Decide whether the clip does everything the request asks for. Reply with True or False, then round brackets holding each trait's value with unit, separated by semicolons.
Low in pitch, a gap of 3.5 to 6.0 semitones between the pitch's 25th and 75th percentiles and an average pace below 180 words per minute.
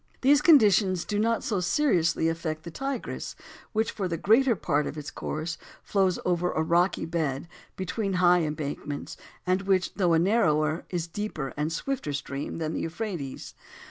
False (175 Hz; 4.6 semitones; 170 wpm)